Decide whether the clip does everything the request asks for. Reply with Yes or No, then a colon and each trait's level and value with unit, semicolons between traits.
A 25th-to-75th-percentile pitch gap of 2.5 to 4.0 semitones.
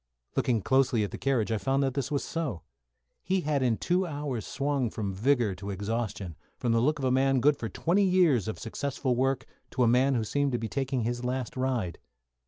Yes: average, 3.7 semitones